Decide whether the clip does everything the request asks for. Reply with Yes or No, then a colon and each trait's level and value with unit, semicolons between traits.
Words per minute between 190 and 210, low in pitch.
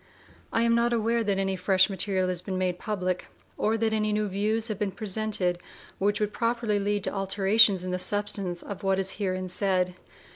No: average, 195 wpm; high, 200 Hz